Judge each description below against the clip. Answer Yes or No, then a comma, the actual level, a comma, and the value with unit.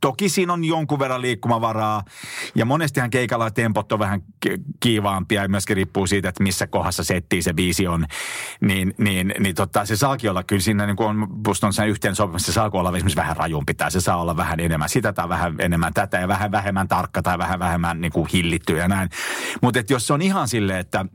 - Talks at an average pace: No, fast, 205 wpm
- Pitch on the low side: Yes, low, 100 Hz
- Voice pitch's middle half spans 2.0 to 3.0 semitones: No, average, 3.5 semitones